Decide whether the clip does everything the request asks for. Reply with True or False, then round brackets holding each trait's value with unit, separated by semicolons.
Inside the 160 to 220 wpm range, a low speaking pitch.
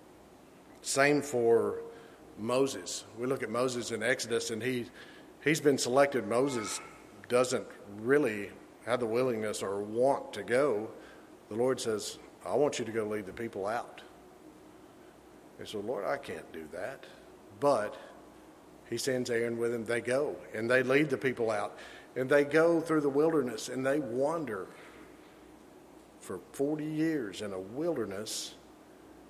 False (145 wpm; 130 Hz)